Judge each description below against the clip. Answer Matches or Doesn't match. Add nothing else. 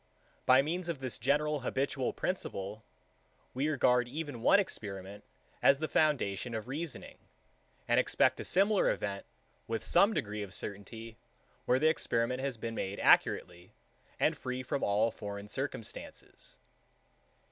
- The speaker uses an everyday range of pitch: Doesn't match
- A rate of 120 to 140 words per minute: Matches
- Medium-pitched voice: Doesn't match